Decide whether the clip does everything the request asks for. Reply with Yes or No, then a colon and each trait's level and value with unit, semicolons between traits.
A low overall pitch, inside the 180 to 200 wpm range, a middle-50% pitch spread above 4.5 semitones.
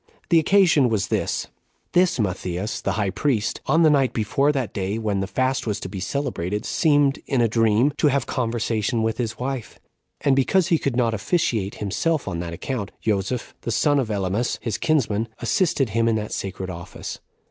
Yes: low, 115 Hz; average, 190 wpm; average, 5.2 semitones